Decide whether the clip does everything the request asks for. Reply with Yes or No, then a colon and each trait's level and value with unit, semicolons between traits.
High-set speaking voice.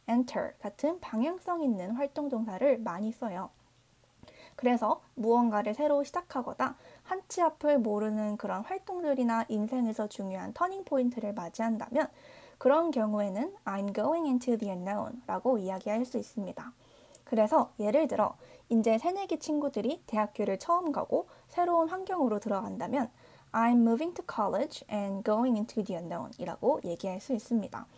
Yes: high, 235 Hz